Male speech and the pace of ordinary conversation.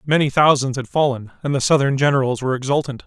Yes: male; average, 195 wpm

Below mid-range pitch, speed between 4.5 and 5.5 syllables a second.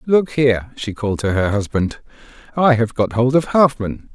Yes: low, 120 Hz; 4.9 syllables/s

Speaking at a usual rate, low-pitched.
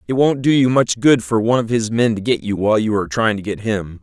No: fast, 315 wpm; low, 110 Hz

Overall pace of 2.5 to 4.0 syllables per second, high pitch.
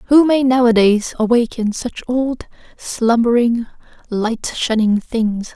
Yes: 3.6 syllables/s; high, 235 Hz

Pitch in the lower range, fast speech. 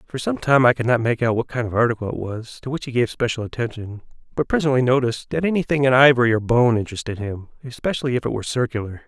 Yes: low, 120 Hz; fast, 240 wpm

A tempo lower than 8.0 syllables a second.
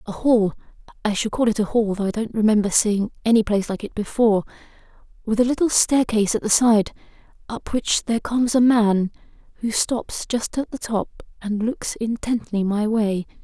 No: 8.7 syllables/s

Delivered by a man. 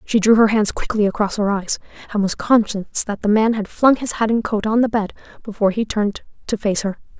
No: female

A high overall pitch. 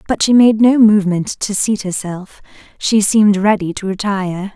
Yes: high, 200 Hz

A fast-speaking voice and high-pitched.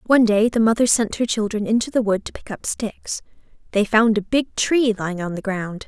Yes: fast, 235 wpm; high, 215 Hz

